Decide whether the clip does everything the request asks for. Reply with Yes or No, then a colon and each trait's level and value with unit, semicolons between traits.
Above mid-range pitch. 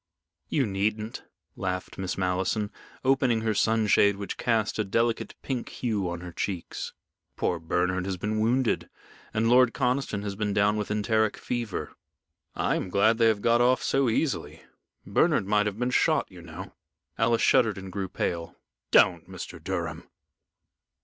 No: low, 105 Hz